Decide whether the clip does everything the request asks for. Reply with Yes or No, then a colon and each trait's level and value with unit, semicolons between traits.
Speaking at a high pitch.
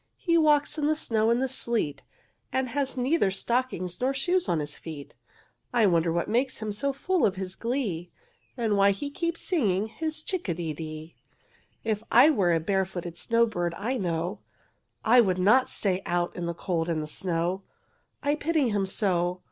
Yes: high, 210 Hz